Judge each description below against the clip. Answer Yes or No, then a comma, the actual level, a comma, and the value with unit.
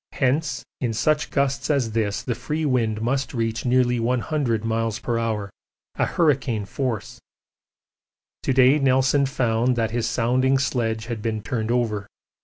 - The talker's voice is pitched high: No, low, 120 Hz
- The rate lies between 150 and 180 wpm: No, average, 140 wpm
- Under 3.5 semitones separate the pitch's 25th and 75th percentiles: Yes, average, 2.9 semitones